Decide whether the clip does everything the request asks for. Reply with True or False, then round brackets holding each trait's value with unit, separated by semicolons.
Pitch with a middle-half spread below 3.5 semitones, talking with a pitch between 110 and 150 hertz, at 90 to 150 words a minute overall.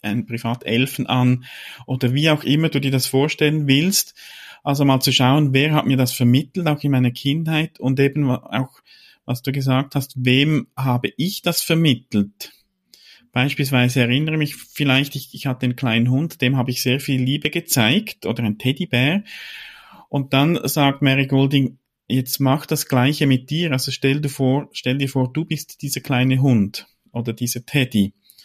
False (2.4 semitones; 135 Hz; 175 wpm)